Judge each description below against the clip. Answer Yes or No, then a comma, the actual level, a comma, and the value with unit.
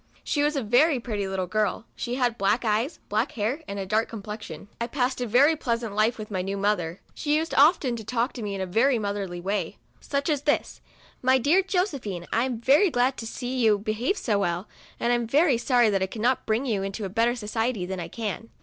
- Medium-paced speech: No, fast, 230 wpm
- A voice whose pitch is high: Yes, high, 230 Hz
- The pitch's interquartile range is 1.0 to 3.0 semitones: No, average, 4.2 semitones